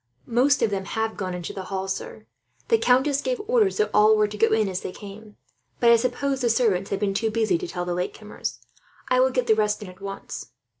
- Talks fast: Yes, fast, 240 wpm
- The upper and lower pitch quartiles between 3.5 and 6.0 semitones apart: Yes, average, 4.2 semitones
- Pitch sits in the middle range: No, high, 215 Hz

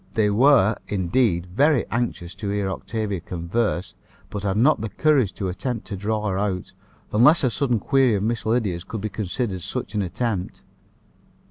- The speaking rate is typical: Yes, average, 170 wpm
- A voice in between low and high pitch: No, low, 105 Hz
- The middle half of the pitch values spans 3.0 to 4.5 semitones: Yes, average, 3.8 semitones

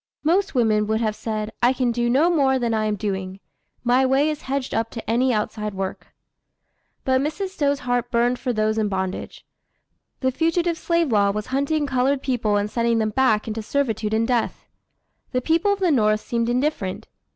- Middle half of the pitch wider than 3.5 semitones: Yes, average, 4.4 semitones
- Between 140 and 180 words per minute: No, average, 190 wpm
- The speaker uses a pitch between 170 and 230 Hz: No, high, 240 Hz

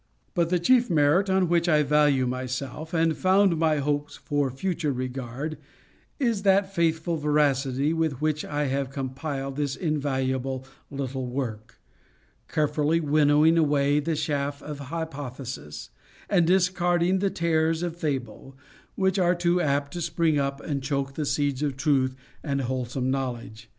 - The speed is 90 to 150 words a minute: Yes, average, 145 wpm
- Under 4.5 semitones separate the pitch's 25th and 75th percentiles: Yes, average, 3.5 semitones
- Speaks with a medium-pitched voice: Yes, medium, 145 Hz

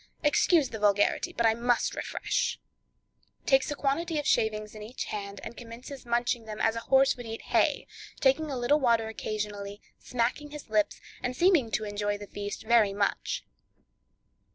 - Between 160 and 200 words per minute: Yes, average, 170 wpm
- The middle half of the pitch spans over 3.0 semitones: Yes, average, 4.1 semitones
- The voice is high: Yes, high, 230 Hz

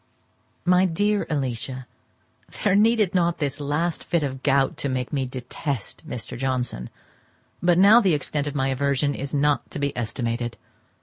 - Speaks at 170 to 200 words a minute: No, average, 160 wpm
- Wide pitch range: No, average, 4.8 semitones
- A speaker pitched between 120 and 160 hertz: Yes, medium, 140 Hz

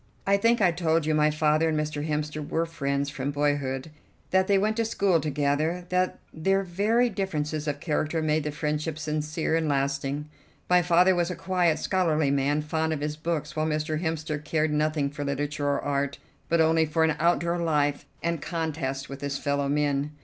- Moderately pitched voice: Yes, medium, 155 Hz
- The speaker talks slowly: No, average, 190 wpm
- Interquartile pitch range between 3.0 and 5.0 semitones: No, narrow, 2.4 semitones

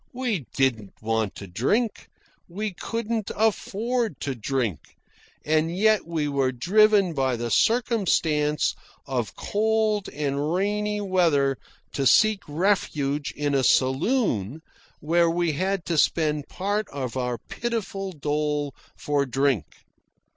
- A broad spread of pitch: Yes, wide, 7.2 semitones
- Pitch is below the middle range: No, medium, 155 Hz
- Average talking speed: No, slow, 120 wpm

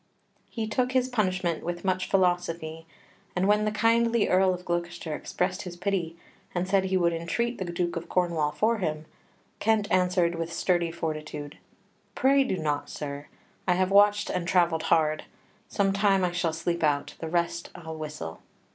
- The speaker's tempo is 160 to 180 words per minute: Yes, average, 170 wpm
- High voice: No, medium, 175 Hz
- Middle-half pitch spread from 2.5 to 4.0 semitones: Yes, average, 3.0 semitones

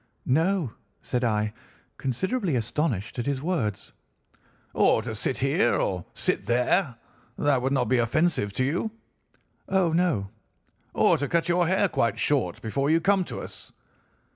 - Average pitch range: No, wide, 6.8 semitones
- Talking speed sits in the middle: Yes, average, 150 wpm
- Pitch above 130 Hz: Yes, medium, 140 Hz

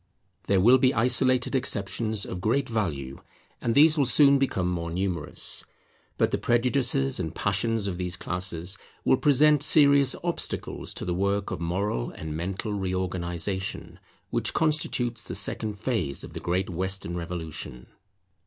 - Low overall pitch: Yes, low, 100 Hz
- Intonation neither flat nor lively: No, wide, 6.0 semitones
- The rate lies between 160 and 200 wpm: No, average, 145 wpm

